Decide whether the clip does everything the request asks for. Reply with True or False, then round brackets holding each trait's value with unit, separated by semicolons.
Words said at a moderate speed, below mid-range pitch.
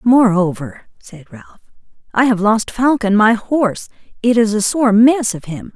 False (165 wpm; 220 Hz)